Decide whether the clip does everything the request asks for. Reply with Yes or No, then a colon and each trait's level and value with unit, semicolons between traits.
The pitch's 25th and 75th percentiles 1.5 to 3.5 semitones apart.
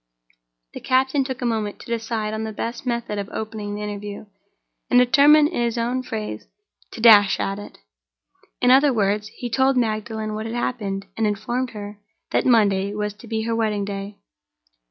Yes: average, 2.8 semitones